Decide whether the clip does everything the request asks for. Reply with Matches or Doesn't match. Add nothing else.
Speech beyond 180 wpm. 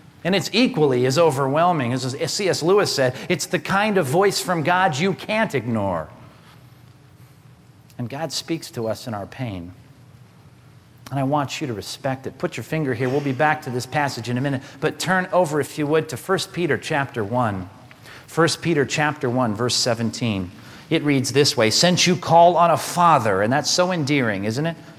Matches